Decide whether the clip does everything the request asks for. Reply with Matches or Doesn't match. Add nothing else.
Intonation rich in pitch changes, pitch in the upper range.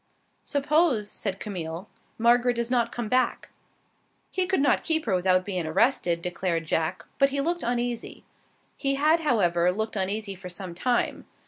Matches